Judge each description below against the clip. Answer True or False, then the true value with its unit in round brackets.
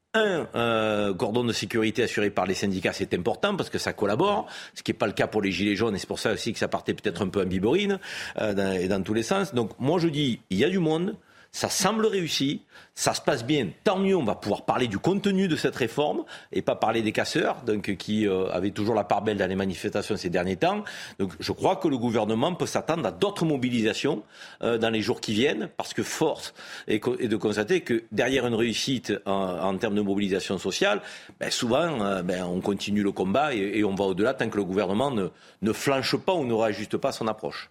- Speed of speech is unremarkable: False (240 wpm)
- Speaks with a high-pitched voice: False (110 Hz)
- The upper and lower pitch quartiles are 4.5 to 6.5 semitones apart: True (5.0 semitones)